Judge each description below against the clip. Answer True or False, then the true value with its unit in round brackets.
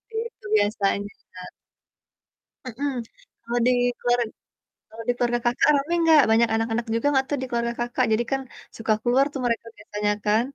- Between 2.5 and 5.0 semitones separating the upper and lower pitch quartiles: True (2.8 semitones)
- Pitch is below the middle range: False (240 Hz)